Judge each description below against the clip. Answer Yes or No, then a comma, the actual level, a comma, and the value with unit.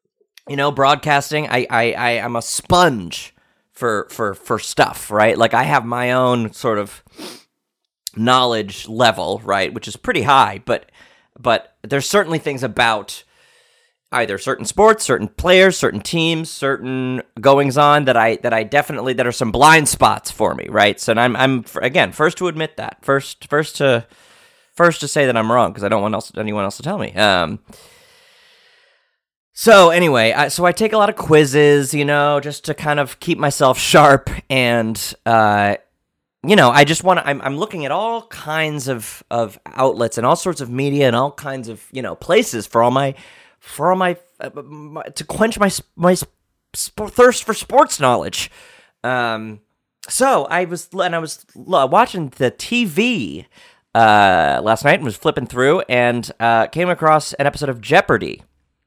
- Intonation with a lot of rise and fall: Yes, wide, 6.2 semitones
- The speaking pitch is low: No, medium, 145 Hz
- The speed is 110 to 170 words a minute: No, average, 180 wpm